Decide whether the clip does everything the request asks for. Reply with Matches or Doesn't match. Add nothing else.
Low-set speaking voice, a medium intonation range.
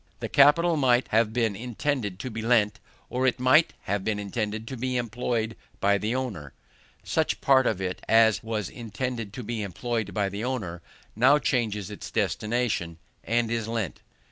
Matches